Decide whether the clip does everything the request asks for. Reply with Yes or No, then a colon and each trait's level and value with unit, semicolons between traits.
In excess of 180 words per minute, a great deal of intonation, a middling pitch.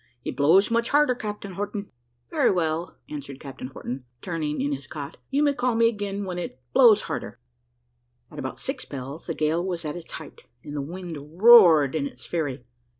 Yes: average, 190 wpm; wide, 6.0 semitones; medium, 170 Hz